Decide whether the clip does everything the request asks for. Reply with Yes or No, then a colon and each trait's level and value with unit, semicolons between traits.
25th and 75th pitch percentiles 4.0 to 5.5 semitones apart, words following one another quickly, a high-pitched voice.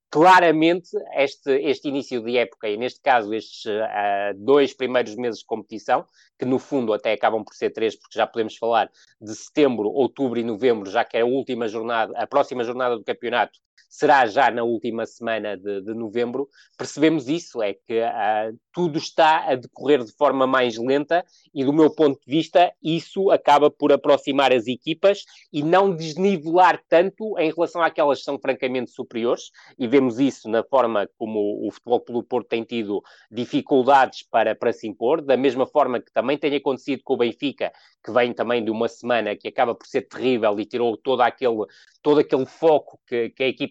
No: average, 5.1 semitones; fast, 190 wpm; low, 130 Hz